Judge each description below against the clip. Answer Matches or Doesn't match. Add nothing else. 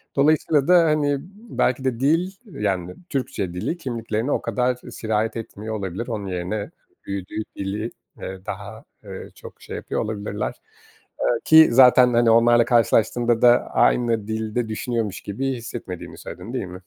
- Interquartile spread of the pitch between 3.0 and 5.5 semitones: Matches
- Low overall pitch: Matches